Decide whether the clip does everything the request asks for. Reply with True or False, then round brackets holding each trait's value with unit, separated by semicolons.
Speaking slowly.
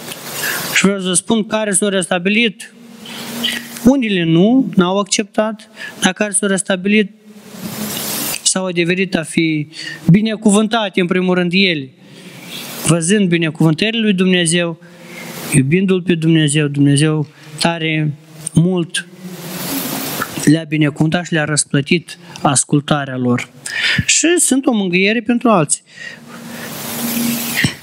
True (105 wpm)